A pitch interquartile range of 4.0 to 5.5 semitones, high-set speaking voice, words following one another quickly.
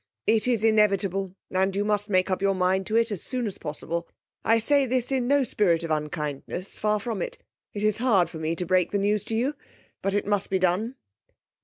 No: average, 3.4 semitones; high, 200 Hz; fast, 220 wpm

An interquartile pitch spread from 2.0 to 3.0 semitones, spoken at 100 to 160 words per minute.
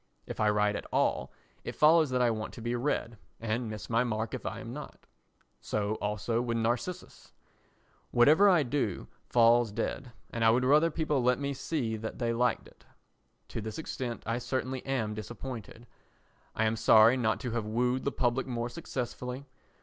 No: average, 2.7 semitones; average, 180 wpm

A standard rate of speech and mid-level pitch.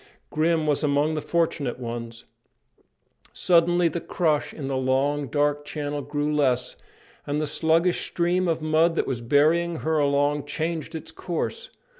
Yes: average, 150 wpm; medium, 150 Hz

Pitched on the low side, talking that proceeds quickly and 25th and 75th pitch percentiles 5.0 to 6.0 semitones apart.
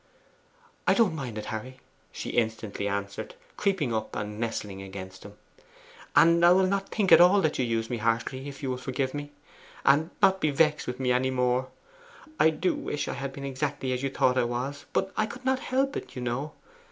Yes: low, 130 Hz; fast, 210 wpm; wide, 5.4 semitones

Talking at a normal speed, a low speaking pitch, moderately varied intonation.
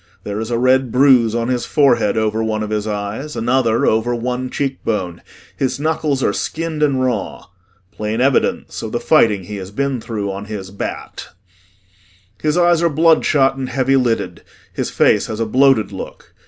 Yes: average, 175 wpm; low, 120 Hz; average, 4.0 semitones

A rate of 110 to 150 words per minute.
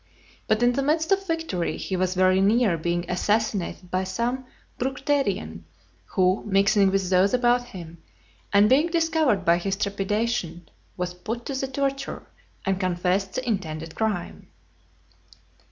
Yes: average, 140 wpm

